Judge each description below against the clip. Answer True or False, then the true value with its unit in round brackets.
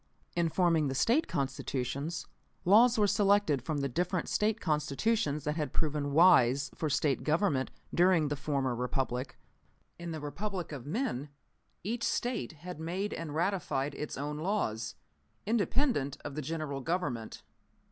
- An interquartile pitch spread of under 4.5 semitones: False (5.1 semitones)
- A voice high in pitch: False (155 Hz)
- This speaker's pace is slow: False (145 wpm)